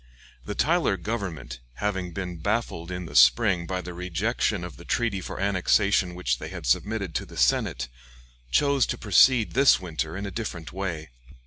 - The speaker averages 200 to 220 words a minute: No, average, 175 wpm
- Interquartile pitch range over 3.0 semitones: Yes, average, 3.9 semitones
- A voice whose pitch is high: No, very low, 90 Hz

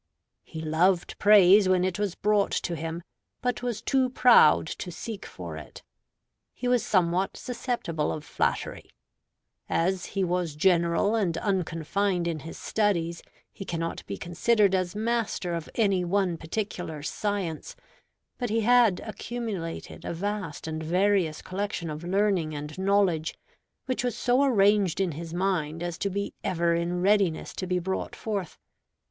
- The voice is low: No, medium, 185 Hz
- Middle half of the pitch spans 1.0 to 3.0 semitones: No, average, 3.7 semitones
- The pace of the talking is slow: No, average, 150 wpm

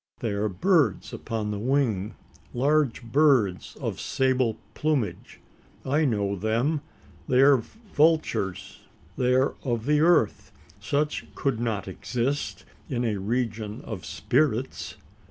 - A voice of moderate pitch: No, low, 125 Hz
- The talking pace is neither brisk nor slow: No, slow, 120 wpm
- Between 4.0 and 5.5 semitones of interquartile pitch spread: Yes, average, 5.1 semitones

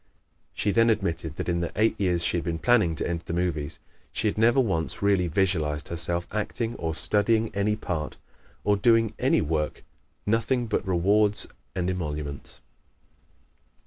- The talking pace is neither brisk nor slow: Yes, average, 160 wpm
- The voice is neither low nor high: No, very low, 90 Hz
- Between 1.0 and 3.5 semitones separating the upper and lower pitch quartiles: No, average, 4.4 semitones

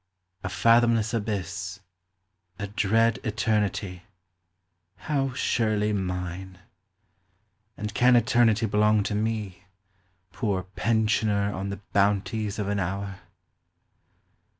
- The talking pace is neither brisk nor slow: No, slow, 95 wpm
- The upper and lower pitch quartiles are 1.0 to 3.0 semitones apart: Yes, narrow, 2.4 semitones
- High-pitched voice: No, low, 105 Hz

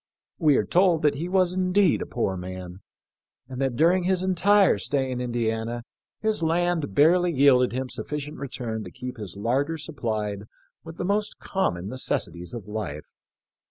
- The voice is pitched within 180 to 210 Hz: No, low, 135 Hz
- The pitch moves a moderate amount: No, wide, 7.7 semitones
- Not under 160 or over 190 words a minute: Yes, average, 165 wpm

